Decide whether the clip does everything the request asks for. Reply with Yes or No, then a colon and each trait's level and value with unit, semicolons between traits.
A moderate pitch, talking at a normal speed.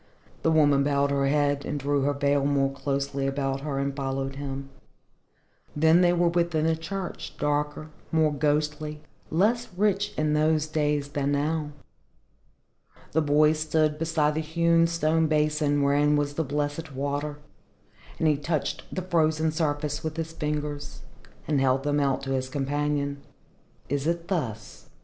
Yes: medium, 150 Hz; average, 155 wpm